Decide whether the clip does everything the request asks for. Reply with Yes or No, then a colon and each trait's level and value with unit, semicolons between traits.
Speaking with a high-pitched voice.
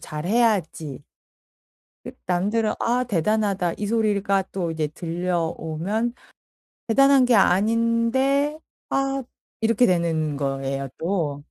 Yes: high, 195 Hz